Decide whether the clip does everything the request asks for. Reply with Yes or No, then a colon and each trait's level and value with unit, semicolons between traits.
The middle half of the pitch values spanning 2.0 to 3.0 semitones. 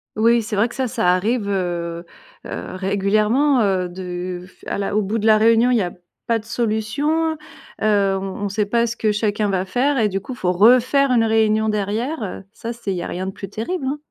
No: average, 3.5 semitones